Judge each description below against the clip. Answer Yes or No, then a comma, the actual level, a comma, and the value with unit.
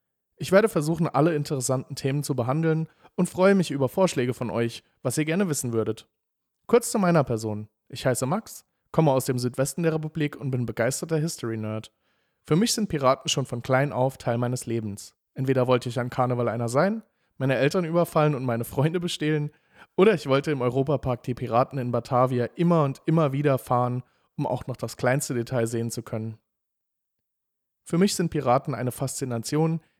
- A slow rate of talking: No, average, 180 wpm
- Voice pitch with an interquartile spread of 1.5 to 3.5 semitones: No, average, 4.5 semitones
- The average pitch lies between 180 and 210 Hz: No, low, 135 Hz